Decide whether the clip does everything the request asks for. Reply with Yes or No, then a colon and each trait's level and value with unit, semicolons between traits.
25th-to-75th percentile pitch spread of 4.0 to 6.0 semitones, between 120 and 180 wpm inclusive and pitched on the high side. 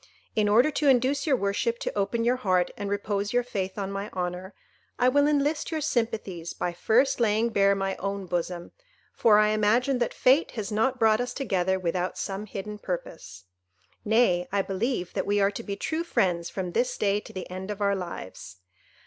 No: average, 4.3 semitones; average, 195 wpm; high, 205 Hz